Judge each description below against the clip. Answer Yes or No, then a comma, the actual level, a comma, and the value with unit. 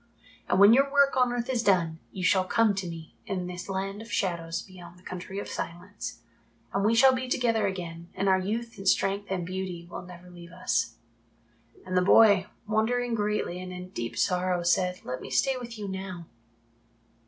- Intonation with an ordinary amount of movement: Yes, average, 3.5 semitones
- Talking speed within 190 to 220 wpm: Yes, average, 195 wpm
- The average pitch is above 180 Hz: Yes, high, 190 Hz